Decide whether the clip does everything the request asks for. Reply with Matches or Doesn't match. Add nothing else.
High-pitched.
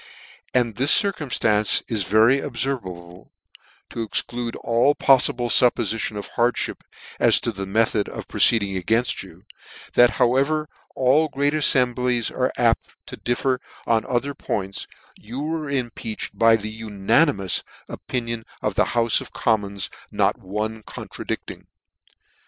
Doesn't match